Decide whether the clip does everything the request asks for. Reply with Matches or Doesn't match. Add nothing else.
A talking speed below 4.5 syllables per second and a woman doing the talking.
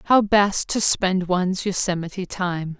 Matches